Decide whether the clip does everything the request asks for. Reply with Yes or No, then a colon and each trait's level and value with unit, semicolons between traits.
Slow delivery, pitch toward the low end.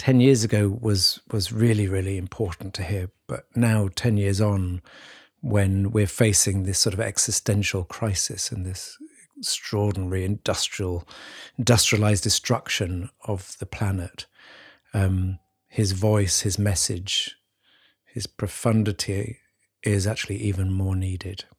Yes: slow, 120 wpm; low, 100 Hz